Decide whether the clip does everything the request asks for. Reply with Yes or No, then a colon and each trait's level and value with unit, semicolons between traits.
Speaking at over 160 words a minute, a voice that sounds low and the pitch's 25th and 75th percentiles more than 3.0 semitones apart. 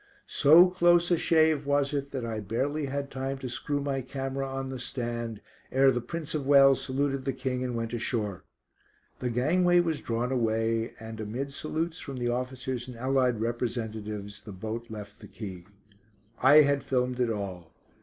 Yes: average, 175 wpm; low, 130 Hz; average, 3.5 semitones